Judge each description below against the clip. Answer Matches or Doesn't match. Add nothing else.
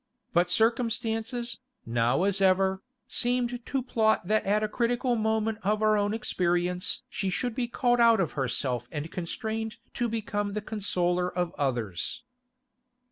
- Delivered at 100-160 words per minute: Matches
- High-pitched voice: Matches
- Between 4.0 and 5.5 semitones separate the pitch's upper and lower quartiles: Matches